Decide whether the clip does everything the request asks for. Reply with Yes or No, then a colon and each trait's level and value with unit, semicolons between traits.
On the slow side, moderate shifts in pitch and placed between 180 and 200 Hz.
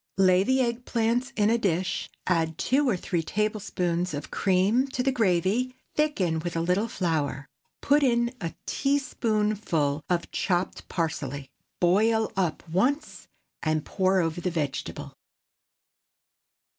No: slow, 130 wpm; wide, 5.9 semitones; high, 190 Hz